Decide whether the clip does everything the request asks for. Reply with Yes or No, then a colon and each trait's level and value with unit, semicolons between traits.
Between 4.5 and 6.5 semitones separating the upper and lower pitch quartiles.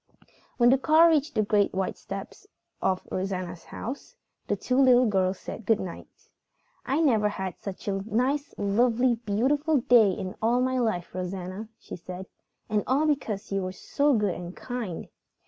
Yes: average, 5.2 semitones